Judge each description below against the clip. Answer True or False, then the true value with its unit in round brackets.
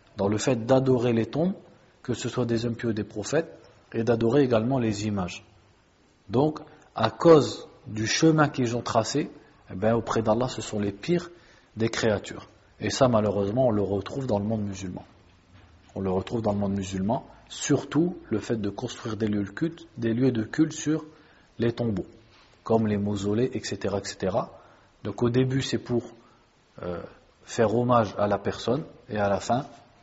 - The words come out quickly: False (180 wpm)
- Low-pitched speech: True (115 Hz)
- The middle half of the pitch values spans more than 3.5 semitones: True (4.0 semitones)